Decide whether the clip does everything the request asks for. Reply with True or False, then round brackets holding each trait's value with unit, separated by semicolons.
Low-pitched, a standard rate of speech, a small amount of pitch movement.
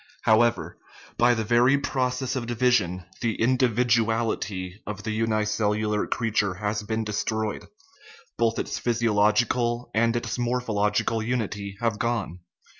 False (115 Hz; 115 wpm; 2.2 semitones)